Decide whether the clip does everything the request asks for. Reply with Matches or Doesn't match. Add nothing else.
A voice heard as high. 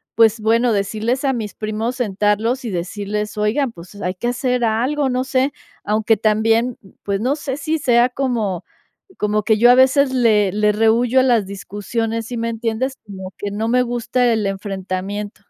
Matches